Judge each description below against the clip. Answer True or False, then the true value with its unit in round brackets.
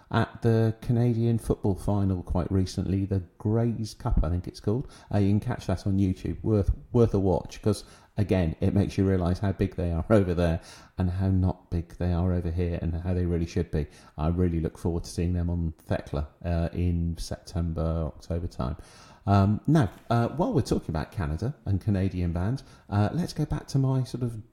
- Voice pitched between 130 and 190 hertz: False (95 Hz)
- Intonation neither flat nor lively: True (4.1 semitones)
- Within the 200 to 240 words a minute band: True (205 wpm)